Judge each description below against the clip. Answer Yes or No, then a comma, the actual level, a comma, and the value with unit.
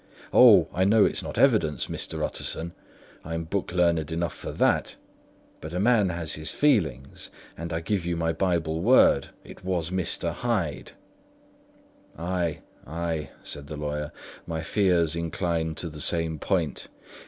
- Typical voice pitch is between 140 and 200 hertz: No, very low, 85 Hz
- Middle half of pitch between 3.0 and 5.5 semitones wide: No, narrow, 2.4 semitones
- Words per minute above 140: Yes, average, 150 wpm